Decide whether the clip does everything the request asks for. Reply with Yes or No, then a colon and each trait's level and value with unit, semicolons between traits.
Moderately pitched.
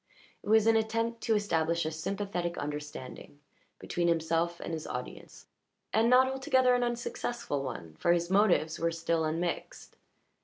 Yes: medium, 175 Hz